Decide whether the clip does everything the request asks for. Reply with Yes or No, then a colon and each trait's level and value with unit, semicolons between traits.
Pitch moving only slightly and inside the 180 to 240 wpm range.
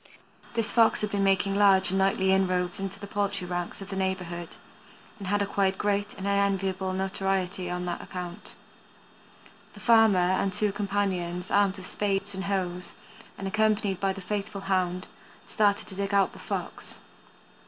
No: narrow, 1.5 semitones; average, 165 wpm